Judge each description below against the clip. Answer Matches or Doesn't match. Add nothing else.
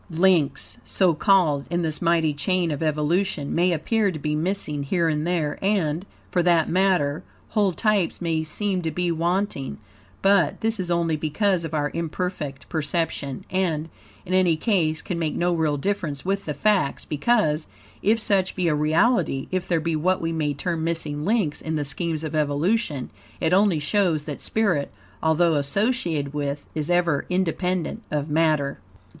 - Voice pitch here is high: Doesn't match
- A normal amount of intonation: Matches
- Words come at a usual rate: Matches